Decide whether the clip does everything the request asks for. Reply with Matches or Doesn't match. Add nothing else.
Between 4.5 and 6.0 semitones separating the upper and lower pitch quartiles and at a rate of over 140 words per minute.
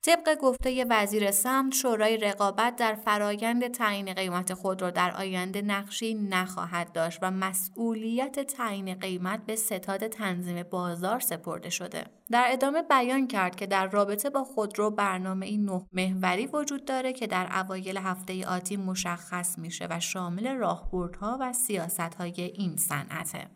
Doesn't match